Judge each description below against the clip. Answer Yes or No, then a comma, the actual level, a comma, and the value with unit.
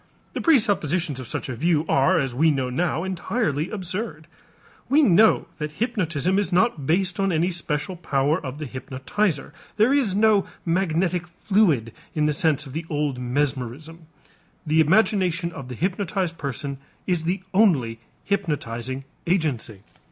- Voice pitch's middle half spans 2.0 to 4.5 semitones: No, average, 5.1 semitones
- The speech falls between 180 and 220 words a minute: No, average, 150 wpm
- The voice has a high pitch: No, medium, 165 Hz